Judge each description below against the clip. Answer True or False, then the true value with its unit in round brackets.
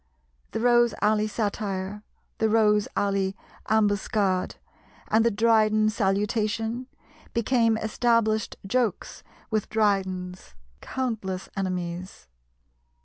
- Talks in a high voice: True (215 Hz)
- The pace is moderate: False (85 wpm)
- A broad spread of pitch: False (2.5 semitones)